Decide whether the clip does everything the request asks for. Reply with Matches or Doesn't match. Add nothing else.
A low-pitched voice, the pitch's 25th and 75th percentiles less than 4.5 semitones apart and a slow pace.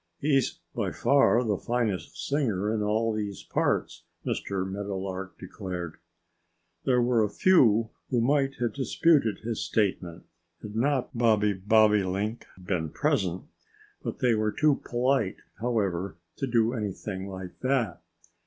Matches